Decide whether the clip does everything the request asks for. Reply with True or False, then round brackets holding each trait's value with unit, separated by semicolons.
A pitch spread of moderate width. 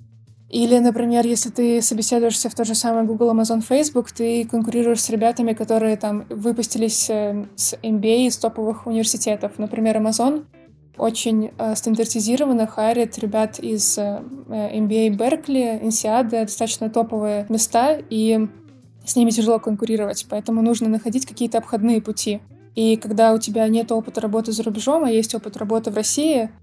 False (1.2 semitones)